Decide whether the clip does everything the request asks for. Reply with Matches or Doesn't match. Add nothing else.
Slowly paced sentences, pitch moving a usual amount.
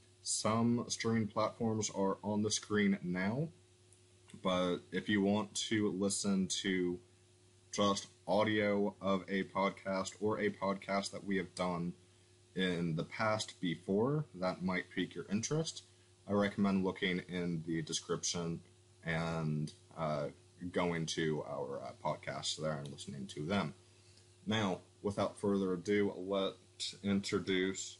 Doesn't match